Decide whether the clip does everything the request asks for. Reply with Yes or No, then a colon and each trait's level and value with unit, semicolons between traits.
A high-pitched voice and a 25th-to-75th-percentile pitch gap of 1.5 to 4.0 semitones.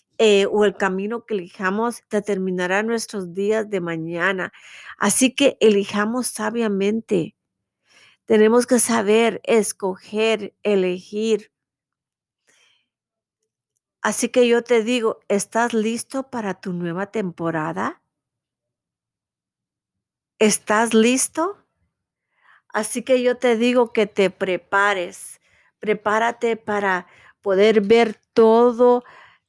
Yes: high, 215 Hz; average, 3.1 semitones